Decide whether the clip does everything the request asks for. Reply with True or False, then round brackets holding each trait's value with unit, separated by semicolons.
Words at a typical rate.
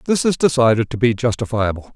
True (185 wpm)